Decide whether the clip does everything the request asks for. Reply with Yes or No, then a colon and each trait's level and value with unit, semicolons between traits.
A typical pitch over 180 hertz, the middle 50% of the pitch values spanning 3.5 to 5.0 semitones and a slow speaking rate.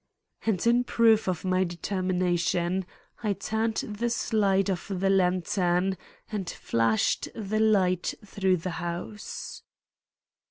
No: high, 190 Hz; average, 3.0 semitones; slow, 115 wpm